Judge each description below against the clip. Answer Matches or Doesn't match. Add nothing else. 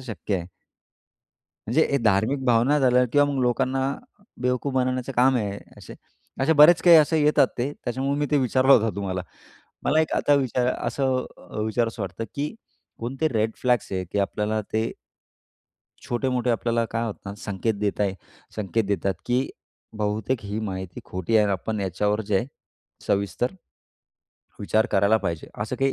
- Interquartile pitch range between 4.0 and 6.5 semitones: Matches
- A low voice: Matches